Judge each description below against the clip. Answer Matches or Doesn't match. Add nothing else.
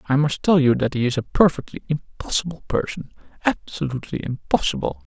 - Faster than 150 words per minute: Doesn't match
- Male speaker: Matches